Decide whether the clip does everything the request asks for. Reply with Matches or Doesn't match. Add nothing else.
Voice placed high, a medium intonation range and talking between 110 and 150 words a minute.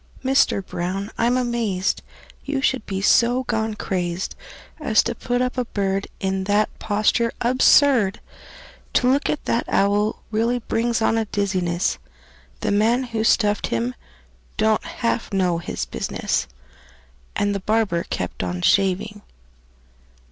Matches